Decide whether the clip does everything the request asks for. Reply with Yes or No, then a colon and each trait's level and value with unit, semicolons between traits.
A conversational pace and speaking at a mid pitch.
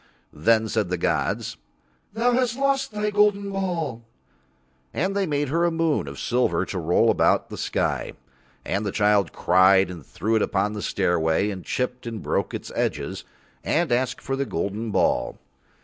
No: average, 170 wpm; low, 120 Hz